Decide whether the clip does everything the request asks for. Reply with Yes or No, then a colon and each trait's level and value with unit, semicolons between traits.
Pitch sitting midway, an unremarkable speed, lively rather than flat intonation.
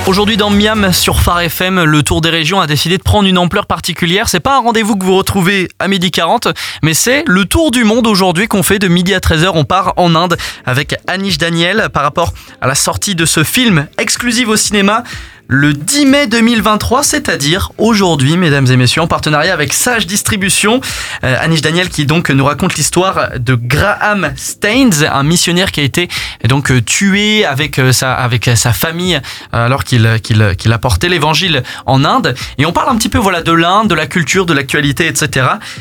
Yes: medium, 175 Hz; average, 195 wpm; wide, 5.7 semitones